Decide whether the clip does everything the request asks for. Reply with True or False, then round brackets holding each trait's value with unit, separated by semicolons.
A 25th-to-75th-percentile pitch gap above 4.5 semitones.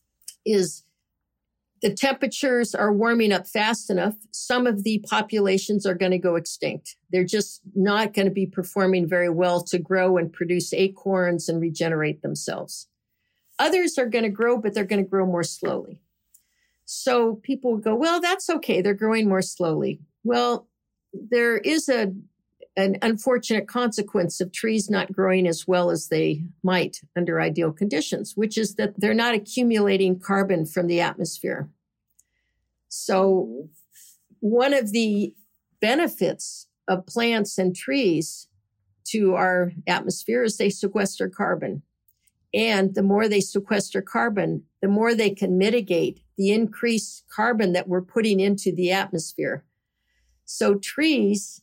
False (3.5 semitones)